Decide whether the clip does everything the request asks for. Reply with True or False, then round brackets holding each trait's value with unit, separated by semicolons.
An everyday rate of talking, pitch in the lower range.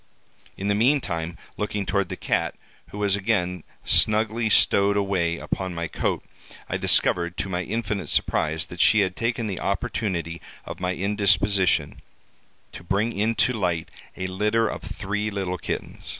True (150 wpm; 100 Hz)